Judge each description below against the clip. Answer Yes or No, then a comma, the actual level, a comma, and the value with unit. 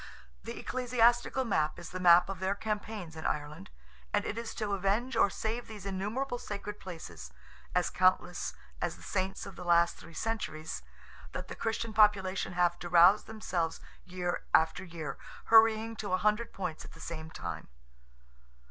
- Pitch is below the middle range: No, high, 190 Hz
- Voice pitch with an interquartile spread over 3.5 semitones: Yes, average, 4.2 semitones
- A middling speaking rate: Yes, average, 160 wpm